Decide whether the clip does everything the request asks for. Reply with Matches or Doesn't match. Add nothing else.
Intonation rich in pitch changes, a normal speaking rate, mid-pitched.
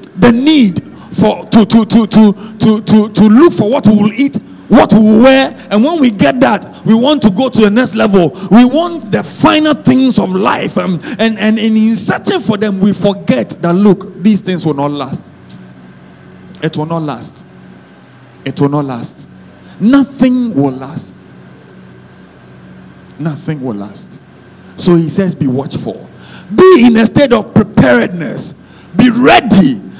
Doesn't match